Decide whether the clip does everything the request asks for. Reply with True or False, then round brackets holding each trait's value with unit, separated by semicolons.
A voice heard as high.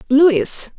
True (275 Hz)